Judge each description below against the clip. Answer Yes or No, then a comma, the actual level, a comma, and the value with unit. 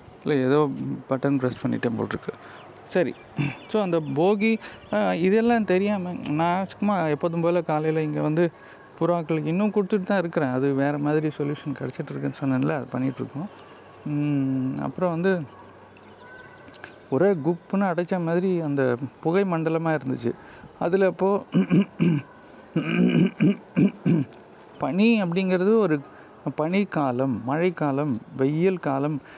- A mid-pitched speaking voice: Yes, medium, 160 Hz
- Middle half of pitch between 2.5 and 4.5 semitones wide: No, average, 5.0 semitones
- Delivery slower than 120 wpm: Yes, average, 105 wpm